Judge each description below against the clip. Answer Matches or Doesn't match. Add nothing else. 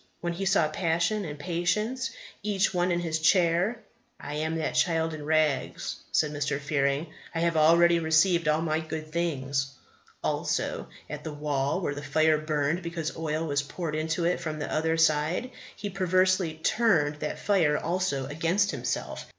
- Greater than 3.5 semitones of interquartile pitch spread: Doesn't match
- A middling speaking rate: Matches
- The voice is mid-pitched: Matches